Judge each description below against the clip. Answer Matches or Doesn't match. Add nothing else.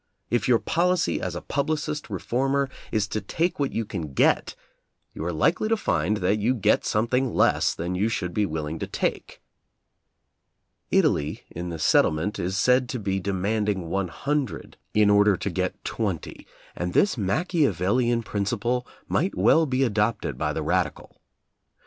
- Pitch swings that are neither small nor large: Doesn't match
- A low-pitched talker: Matches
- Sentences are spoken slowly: Doesn't match